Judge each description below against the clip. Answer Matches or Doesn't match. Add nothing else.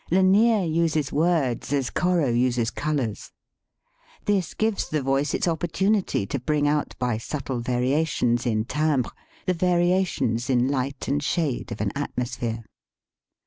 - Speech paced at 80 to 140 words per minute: Matches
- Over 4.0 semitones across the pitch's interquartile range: Matches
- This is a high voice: Doesn't match